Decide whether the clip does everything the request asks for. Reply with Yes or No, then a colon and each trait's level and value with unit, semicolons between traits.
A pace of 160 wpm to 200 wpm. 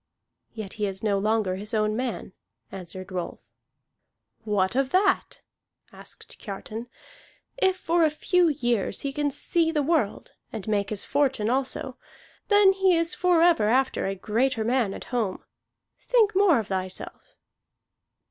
No: average, 145 wpm